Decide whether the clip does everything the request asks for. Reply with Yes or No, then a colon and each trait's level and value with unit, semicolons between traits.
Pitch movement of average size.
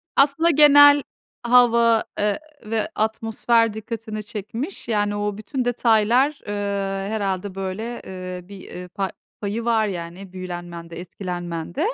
Yes: average, 3.7 semitones